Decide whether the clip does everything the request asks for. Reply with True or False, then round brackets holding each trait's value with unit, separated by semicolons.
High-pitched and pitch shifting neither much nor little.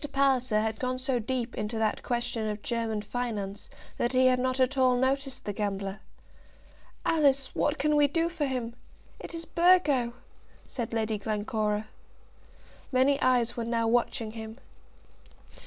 True (245 Hz; 3.3 semitones)